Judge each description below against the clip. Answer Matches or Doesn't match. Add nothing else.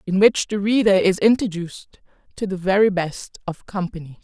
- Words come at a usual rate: Matches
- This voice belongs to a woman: Matches